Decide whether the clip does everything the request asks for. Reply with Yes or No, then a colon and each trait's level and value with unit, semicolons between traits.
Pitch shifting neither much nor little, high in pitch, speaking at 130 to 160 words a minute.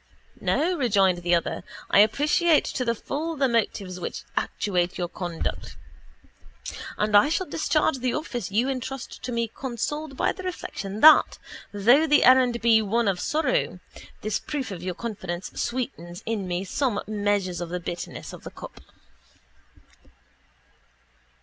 No: wide, 6.1 semitones; high, 230 Hz; average, 145 wpm